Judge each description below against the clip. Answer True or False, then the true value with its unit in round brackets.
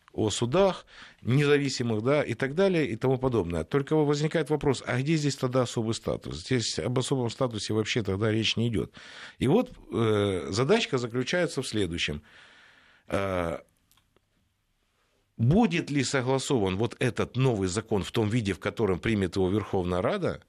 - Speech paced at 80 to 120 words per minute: False (145 wpm)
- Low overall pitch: True (120 Hz)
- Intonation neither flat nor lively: True (5.0 semitones)